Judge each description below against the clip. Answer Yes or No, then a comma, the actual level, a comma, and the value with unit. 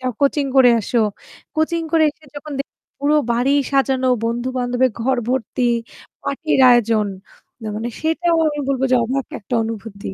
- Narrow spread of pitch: No, average, 3.2 semitones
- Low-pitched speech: No, very high, 260 Hz